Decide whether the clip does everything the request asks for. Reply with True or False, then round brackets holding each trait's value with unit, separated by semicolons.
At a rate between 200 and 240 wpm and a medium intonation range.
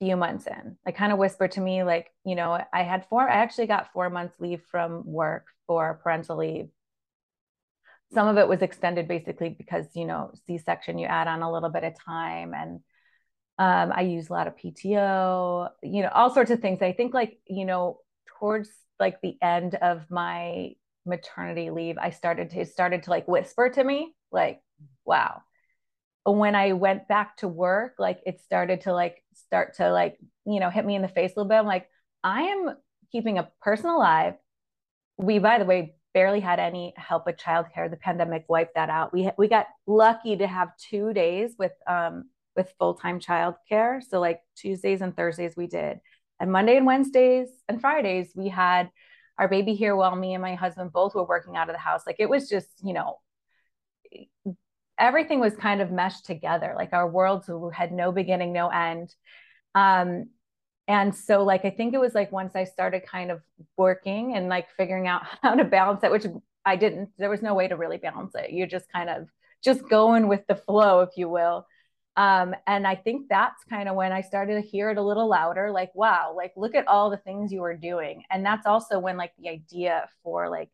True (205 wpm; 3.0 semitones)